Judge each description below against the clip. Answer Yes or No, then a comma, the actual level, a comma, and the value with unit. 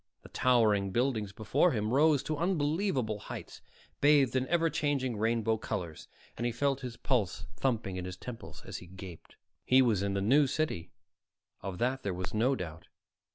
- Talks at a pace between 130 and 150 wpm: No, average, 175 wpm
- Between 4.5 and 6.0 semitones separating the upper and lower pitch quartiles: Yes, wide, 5.5 semitones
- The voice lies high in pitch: No, low, 120 Hz